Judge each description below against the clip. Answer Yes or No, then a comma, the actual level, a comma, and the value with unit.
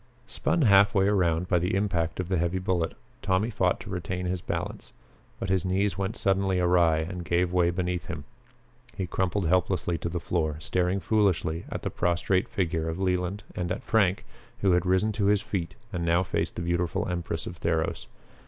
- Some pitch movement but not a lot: No, narrow, 2.0 semitones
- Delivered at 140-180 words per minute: No, average, 190 wpm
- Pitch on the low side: Yes, very low, 90 Hz